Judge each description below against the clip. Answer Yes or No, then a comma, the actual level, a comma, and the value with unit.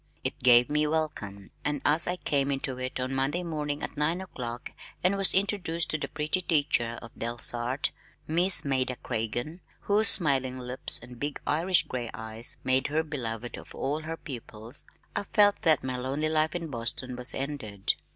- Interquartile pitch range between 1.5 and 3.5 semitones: No, average, 4.3 semitones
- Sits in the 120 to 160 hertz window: Yes, medium, 140 Hz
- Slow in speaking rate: No, average, 175 wpm